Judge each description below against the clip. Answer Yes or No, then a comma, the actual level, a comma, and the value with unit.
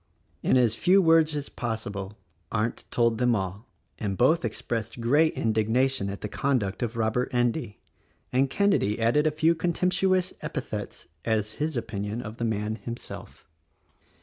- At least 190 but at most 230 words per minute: No, average, 150 wpm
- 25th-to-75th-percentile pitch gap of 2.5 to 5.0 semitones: No, wide, 5.5 semitones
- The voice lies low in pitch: Yes, low, 120 Hz